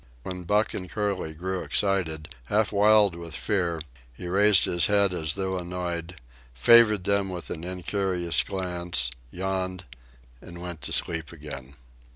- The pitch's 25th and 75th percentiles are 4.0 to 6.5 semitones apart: No, narrow, 2.6 semitones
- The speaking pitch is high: No, very low, 90 Hz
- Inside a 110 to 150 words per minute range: Yes, average, 145 wpm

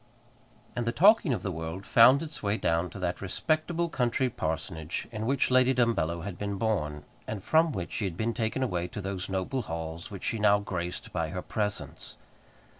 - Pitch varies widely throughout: Yes, wide, 5.7 semitones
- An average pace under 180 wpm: No, average, 190 wpm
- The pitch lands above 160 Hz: No, low, 100 Hz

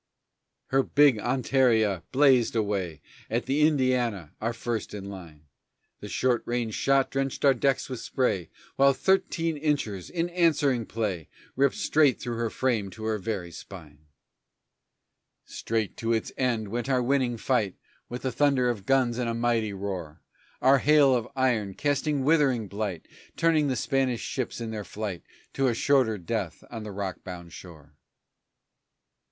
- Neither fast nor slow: Yes, average, 160 wpm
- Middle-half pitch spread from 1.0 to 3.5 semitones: No, average, 4.7 semitones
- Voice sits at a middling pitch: No, low, 120 Hz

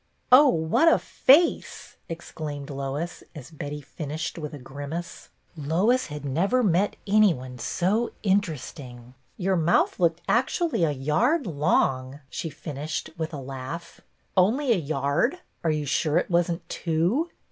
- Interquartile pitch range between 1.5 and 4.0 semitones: No, average, 5.2 semitones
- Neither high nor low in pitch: Yes, medium, 160 Hz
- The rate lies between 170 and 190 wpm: No, average, 160 wpm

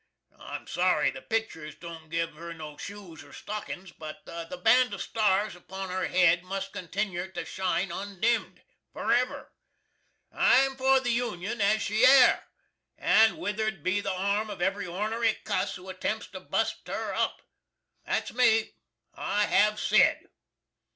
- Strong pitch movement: No, average, 3.5 semitones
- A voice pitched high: Yes, high, 195 Hz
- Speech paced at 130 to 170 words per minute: Yes, average, 150 wpm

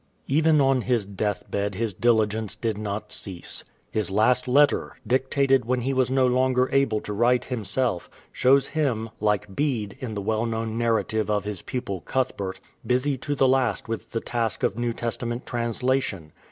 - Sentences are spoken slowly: No, average, 175 wpm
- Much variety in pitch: No, average, 3.4 semitones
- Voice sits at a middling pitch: No, low, 115 Hz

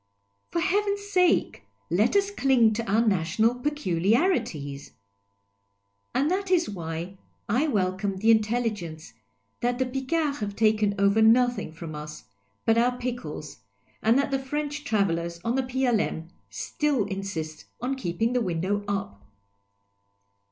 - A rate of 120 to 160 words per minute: Yes, slow, 135 wpm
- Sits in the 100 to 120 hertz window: No, high, 225 Hz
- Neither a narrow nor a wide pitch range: No, wide, 6.1 semitones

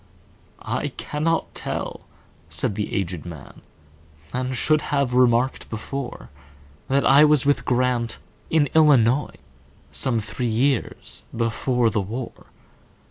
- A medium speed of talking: No, slow, 95 wpm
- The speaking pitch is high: No, low, 120 Hz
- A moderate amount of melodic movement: No, wide, 7.4 semitones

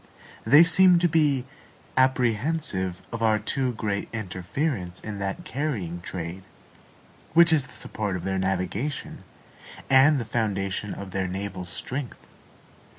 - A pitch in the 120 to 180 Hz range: No, low, 110 Hz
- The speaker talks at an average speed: No, slow, 130 wpm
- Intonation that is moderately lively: No, wide, 6.6 semitones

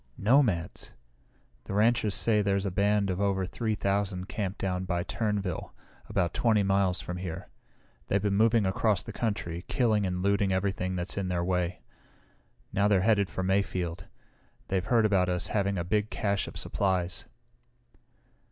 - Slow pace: No, average, 160 wpm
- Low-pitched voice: Yes, low, 100 Hz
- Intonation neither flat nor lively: No, narrow, 2.2 semitones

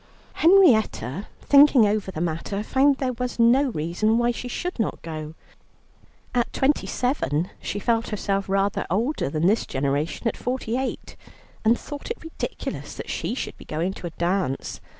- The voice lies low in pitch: No, high, 220 Hz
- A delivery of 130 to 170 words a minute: Yes, average, 165 wpm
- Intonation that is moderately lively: No, wide, 6.6 semitones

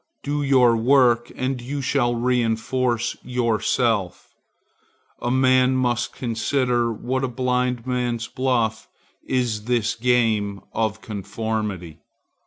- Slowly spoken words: Yes, slow, 100 wpm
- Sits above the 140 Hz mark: No, low, 120 Hz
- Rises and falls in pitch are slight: Yes, narrow, 2.3 semitones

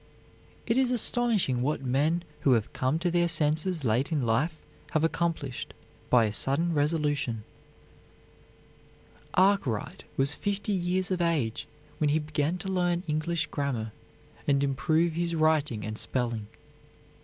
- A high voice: No, medium, 155 Hz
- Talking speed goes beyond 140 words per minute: No, slow, 135 wpm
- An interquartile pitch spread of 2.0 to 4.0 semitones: No, average, 4.4 semitones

